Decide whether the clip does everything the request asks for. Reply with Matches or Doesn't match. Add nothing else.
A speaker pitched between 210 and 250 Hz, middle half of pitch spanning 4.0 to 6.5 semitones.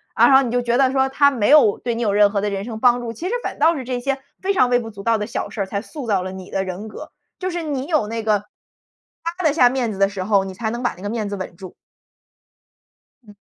Matches